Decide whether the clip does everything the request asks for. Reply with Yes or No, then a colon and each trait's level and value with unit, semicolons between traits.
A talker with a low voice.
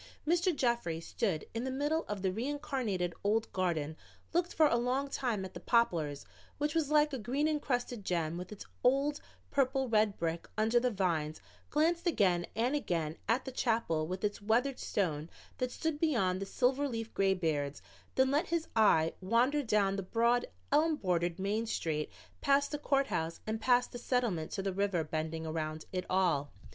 No: high, 220 Hz